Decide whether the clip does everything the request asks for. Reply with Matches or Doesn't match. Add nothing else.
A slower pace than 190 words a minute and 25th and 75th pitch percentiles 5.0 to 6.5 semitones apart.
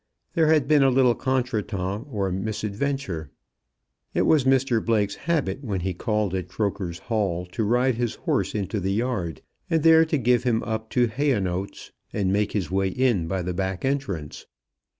Matches